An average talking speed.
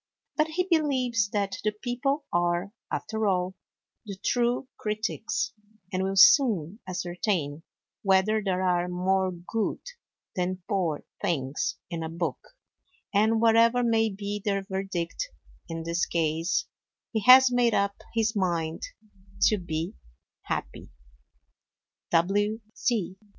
No: slow, 115 wpm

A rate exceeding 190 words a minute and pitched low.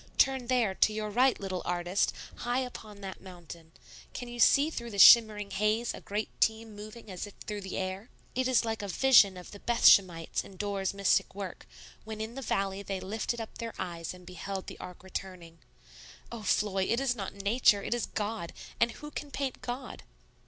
No: average, 200 wpm; high, 210 Hz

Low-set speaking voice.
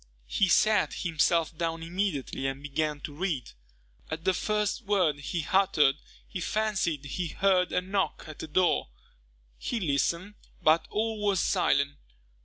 No: medium, 170 Hz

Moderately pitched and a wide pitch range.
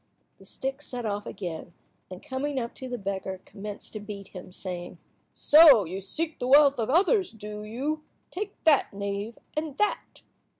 No: high, 230 Hz; wide, 6.6 semitones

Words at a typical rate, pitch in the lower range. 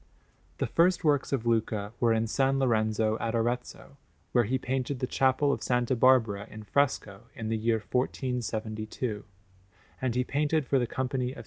Yes: average, 175 wpm; low, 125 Hz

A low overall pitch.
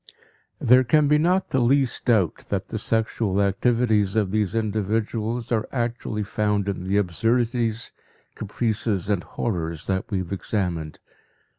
Yes: low, 110 Hz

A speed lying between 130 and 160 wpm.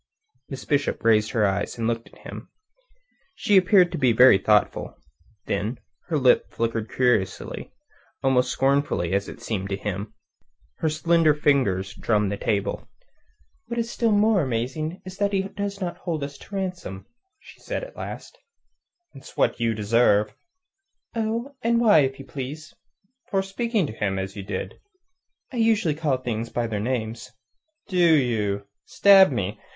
Yes: average, 155 wpm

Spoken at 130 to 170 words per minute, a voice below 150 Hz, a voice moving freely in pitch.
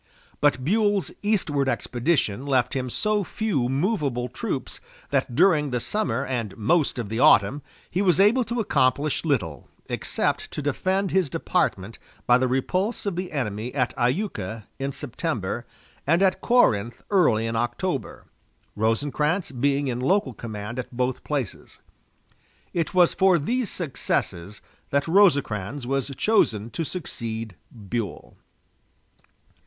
Yes: slow, 135 wpm; low, 135 Hz; wide, 7.3 semitones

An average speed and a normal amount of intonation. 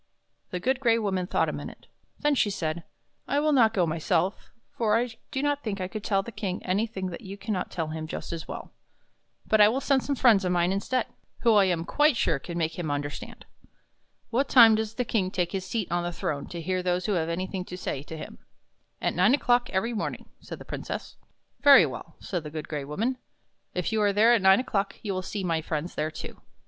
No: fast, 240 wpm; average, 4.9 semitones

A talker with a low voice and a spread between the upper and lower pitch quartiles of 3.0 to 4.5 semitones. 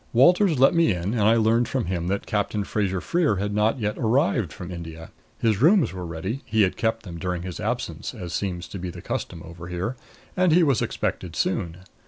No: low, 105 Hz; average, 5.3 semitones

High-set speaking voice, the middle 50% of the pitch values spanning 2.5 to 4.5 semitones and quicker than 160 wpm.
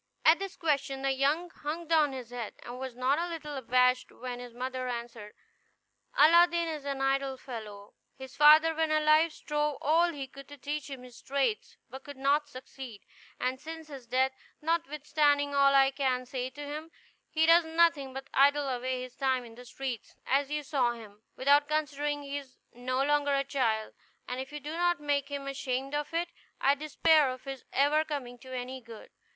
Yes: very high, 275 Hz; average, 2.8 semitones; average, 190 wpm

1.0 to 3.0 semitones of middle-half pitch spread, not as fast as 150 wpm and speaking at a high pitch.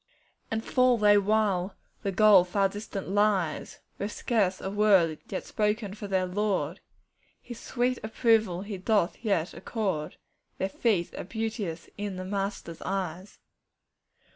Yes: narrow, 2.6 semitones; average, 140 wpm; high, 200 Hz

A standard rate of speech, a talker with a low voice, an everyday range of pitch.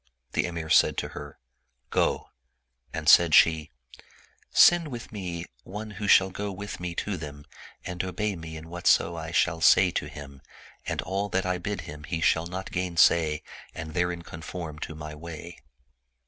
Yes: average, 180 wpm; very low, 85 Hz; average, 3.0 semitones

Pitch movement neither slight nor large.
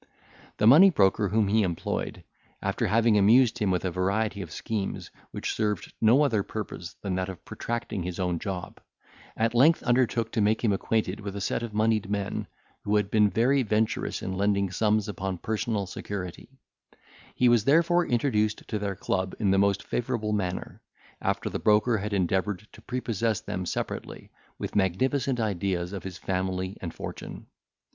Yes: average, 3.0 semitones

